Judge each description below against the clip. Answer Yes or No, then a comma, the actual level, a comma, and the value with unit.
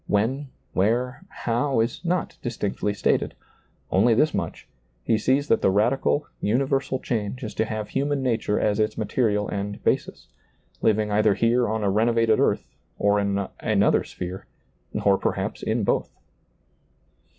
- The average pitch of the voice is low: Yes, low, 110 Hz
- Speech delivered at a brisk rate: No, average, 155 wpm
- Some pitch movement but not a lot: Yes, average, 3.6 semitones